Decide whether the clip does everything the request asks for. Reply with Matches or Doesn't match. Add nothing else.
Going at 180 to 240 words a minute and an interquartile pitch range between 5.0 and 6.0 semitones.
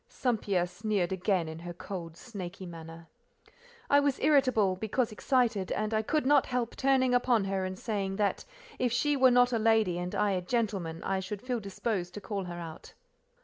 Matches